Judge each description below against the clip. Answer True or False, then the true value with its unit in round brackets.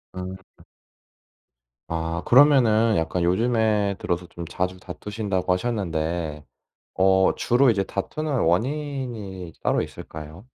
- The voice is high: False (95 Hz)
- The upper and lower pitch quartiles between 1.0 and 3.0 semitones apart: False (4.8 semitones)